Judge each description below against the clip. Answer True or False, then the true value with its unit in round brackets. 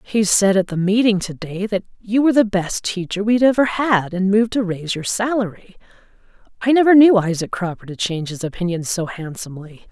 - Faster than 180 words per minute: True (200 wpm)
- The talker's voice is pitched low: False (200 Hz)